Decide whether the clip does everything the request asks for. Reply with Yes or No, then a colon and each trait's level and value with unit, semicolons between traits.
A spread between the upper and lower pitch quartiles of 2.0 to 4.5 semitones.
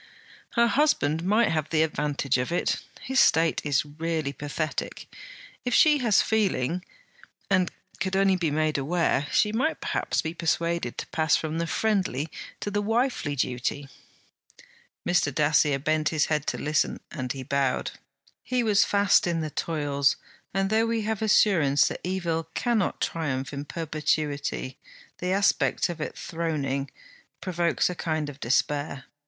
No: average, 4.9 semitones